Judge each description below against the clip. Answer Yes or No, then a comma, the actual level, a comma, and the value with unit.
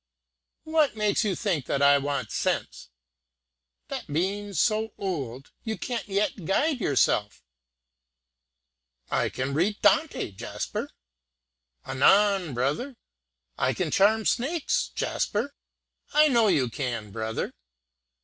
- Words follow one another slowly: Yes, slow, 110 wpm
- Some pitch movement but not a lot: No, wide, 8.3 semitones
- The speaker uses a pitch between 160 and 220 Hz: Yes, high, 190 Hz